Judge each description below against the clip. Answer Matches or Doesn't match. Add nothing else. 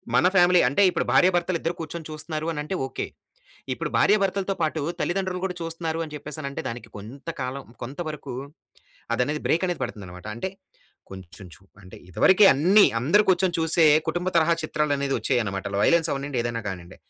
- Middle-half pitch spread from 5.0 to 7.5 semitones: Matches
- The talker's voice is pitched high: Doesn't match